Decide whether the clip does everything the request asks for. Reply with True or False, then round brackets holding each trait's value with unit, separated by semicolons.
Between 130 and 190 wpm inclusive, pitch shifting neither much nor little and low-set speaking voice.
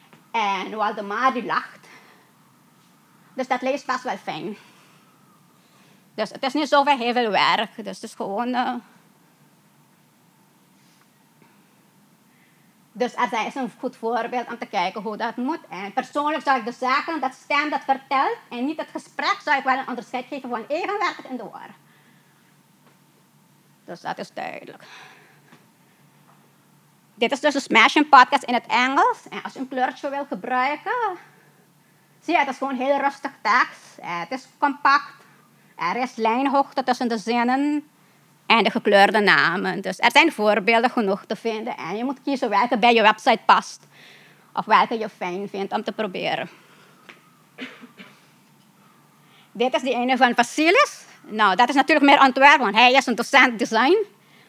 False (155 wpm; 4.2 semitones; 250 Hz)